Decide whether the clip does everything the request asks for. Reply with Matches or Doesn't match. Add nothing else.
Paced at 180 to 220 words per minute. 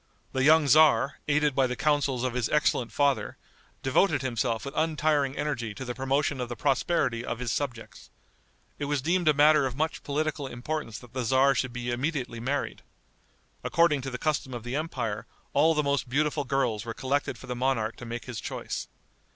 Matches